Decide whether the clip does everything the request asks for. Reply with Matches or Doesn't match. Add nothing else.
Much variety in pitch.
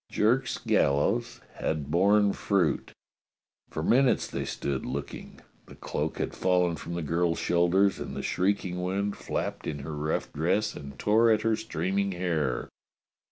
Doesn't match